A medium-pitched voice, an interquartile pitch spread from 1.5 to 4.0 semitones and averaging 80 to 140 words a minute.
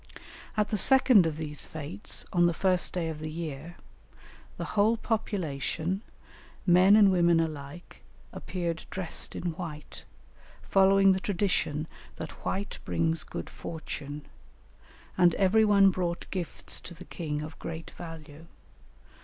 Yes: medium, 175 Hz; average, 3.4 semitones; slow, 135 wpm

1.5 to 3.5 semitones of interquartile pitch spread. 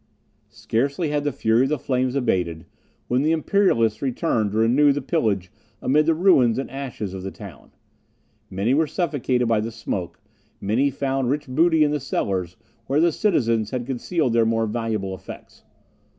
No: average, 4.8 semitones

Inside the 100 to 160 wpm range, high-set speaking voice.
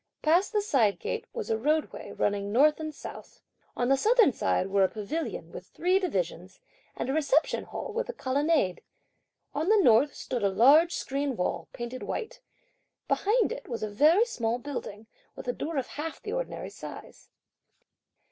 No: average, 175 wpm; very high, 285 Hz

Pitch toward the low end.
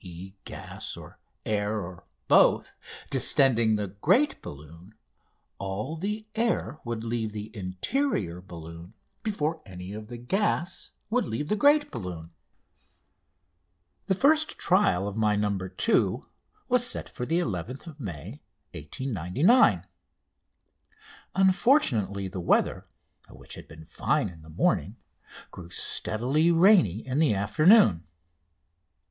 Yes: low, 110 Hz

